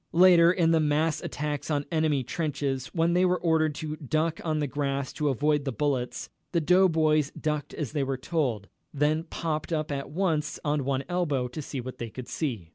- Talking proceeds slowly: No, average, 200 wpm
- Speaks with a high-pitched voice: No, medium, 150 Hz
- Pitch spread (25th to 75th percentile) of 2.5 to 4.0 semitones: Yes, average, 2.8 semitones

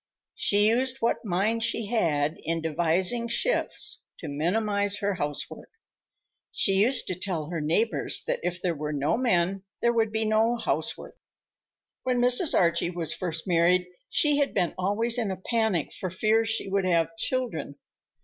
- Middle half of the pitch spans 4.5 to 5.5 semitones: Yes, average, 5.0 semitones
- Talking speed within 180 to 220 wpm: No, average, 160 wpm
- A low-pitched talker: No, high, 195 Hz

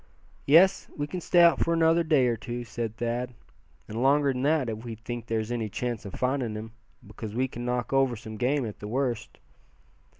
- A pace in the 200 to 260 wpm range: Yes, fast, 205 wpm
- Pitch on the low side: Yes, low, 120 Hz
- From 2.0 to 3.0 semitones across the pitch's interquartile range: No, average, 3.6 semitones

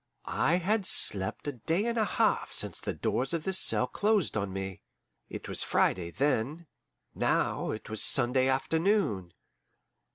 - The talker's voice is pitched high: No, medium, 140 Hz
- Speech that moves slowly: No, average, 155 wpm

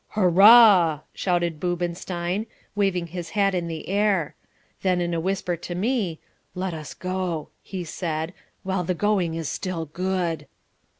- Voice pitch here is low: No, medium, 180 Hz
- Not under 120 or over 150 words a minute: Yes, average, 140 wpm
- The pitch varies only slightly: Yes, narrow, 2.2 semitones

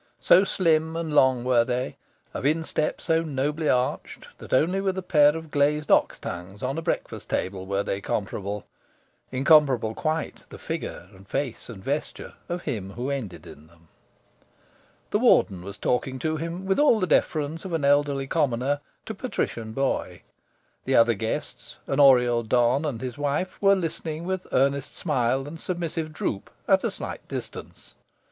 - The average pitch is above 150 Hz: No, medium, 140 Hz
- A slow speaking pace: No, average, 165 wpm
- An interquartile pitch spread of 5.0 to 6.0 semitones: Yes, wide, 5.4 semitones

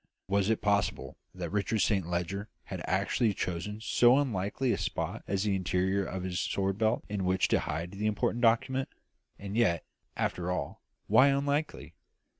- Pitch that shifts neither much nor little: Yes, average, 3.5 semitones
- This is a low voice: Yes, low, 100 Hz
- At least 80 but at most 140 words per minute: No, average, 165 wpm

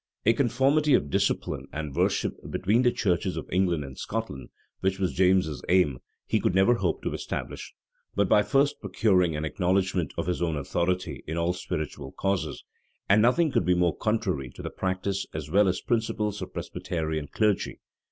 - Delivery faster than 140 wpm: Yes, average, 180 wpm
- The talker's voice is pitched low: Yes, very low, 95 Hz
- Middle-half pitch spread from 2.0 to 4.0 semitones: No, average, 4.5 semitones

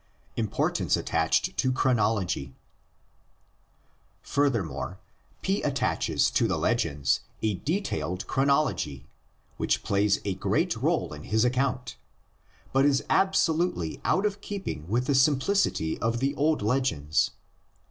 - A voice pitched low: Yes, low, 125 Hz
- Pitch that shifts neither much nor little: No, wide, 6.9 semitones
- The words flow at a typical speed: No, slow, 115 wpm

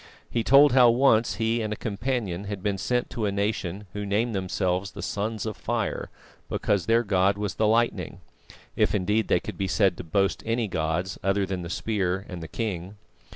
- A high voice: No, low, 105 Hz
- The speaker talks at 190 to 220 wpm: Yes, average, 200 wpm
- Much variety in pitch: No, average, 3.0 semitones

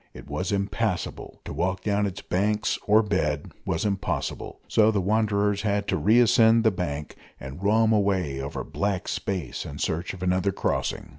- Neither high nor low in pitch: No, low, 100 Hz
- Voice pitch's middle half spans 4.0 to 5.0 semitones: No, average, 2.8 semitones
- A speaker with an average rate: Yes, average, 170 wpm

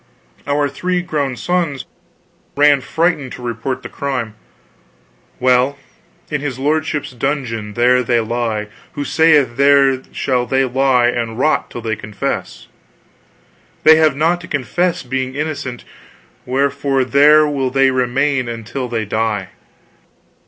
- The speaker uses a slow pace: Yes, slow, 130 wpm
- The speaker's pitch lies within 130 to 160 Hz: Yes, low, 135 Hz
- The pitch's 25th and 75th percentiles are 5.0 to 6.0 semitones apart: No, average, 3.1 semitones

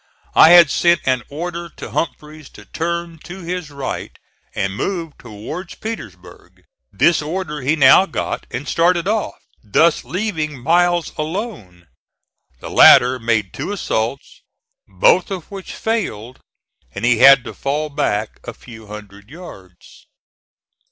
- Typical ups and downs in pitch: No, wide, 6.7 semitones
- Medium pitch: Yes, medium, 155 Hz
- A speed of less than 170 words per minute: Yes, slow, 135 wpm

